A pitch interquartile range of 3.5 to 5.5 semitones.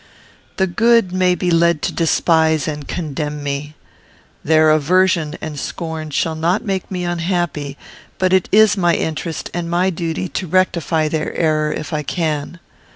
No: average, 2.8 semitones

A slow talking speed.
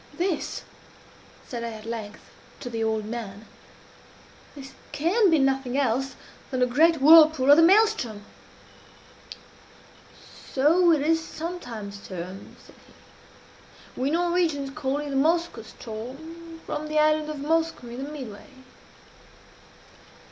Yes: slow, 125 wpm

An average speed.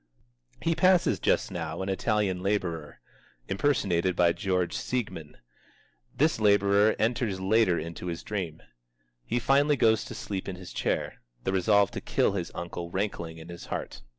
Yes: average, 150 wpm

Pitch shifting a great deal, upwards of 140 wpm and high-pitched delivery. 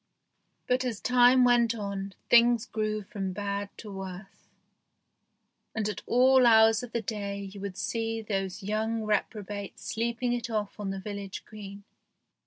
No: average, 2.7 semitones; average, 150 wpm; high, 215 Hz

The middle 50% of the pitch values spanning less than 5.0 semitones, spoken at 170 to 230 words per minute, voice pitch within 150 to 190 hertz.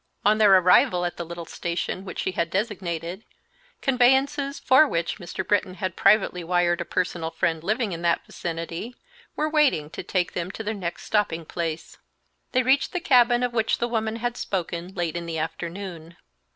No: wide, 5.5 semitones; average, 180 wpm; medium, 185 Hz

